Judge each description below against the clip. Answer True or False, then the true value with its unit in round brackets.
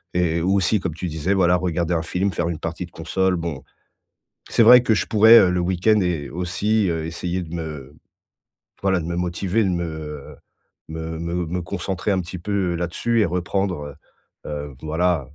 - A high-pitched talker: False (90 Hz)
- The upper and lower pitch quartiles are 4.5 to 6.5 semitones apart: False (2.5 semitones)